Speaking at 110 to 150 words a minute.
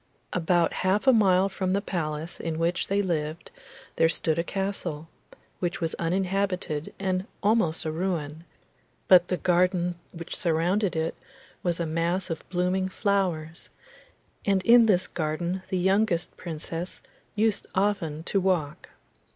Yes: average, 140 wpm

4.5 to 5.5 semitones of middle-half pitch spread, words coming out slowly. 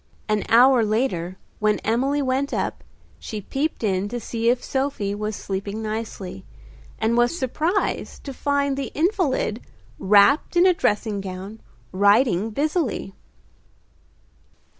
Yes: average, 5.1 semitones; slow, 125 wpm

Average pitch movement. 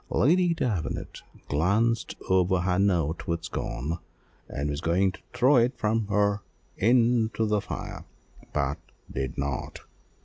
No: wide, 5.9 semitones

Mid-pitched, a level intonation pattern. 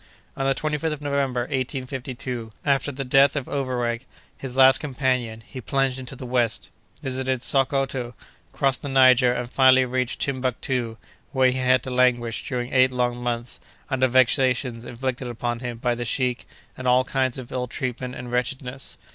No: low, 130 Hz; narrow, 1.4 semitones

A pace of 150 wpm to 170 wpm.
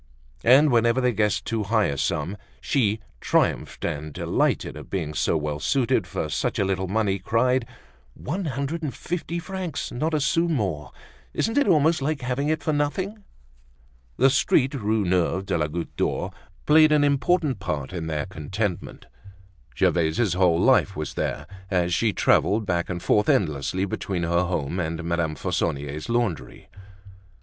Yes: average, 160 wpm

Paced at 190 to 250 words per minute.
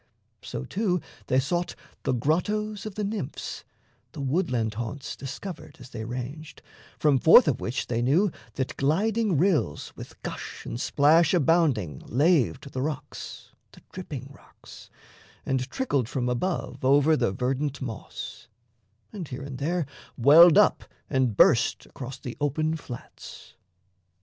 No: average, 140 wpm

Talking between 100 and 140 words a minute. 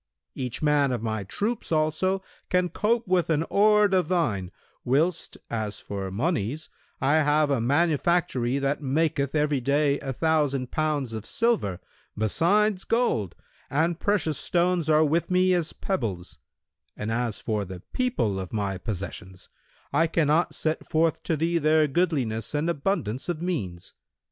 No: average, 150 wpm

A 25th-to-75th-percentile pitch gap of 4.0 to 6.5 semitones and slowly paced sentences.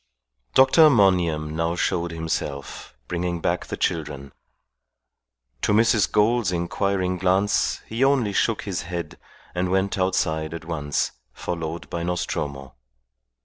No: average, 3.5 semitones; slow, 120 wpm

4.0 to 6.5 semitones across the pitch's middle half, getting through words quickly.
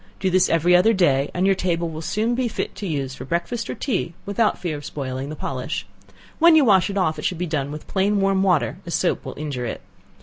Yes: average, 4.7 semitones; fast, 245 wpm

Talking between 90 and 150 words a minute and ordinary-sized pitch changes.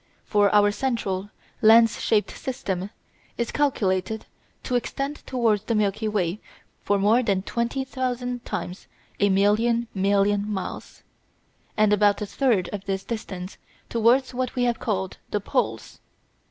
Yes: average, 140 wpm; average, 3.1 semitones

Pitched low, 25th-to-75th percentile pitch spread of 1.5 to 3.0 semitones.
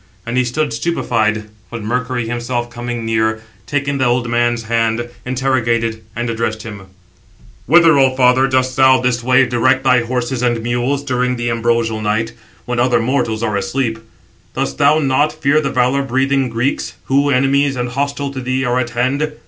Yes: low, 125 Hz; narrow, 2.4 semitones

